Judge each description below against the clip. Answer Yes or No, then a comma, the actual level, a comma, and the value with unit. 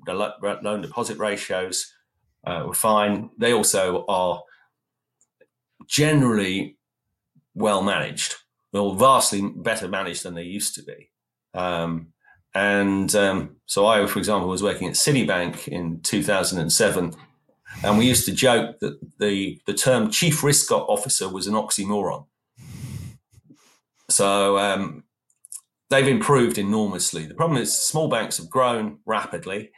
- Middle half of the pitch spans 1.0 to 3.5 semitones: Yes, average, 2.7 semitones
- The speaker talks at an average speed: No, slow, 130 wpm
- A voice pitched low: Yes, low, 100 Hz